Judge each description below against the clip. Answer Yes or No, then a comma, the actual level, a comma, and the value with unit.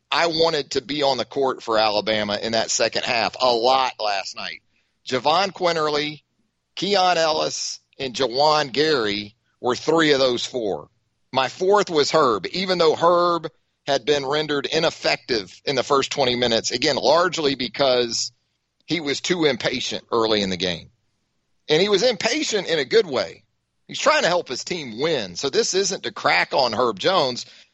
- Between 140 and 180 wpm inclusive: Yes, average, 170 wpm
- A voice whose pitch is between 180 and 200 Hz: No, medium, 140 Hz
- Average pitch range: No, wide, 6.7 semitones